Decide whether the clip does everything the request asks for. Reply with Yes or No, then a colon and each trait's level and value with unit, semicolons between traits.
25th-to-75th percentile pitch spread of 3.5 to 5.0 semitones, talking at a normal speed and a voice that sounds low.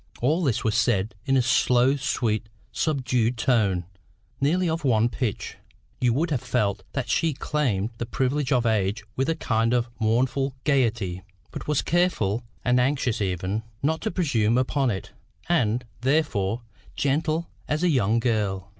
Yes: average, 4.5 semitones; average, 155 wpm; low, 125 Hz